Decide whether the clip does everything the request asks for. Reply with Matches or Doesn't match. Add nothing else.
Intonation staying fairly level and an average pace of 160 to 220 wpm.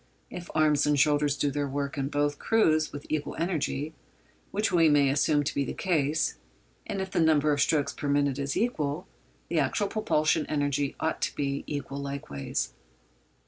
Matches